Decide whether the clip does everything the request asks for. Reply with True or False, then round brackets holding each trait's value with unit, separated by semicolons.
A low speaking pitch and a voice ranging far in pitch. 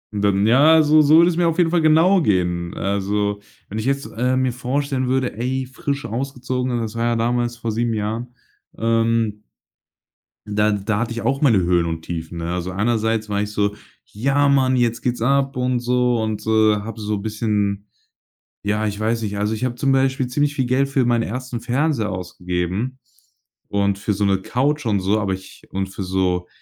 False (115 Hz; 4.1 semitones)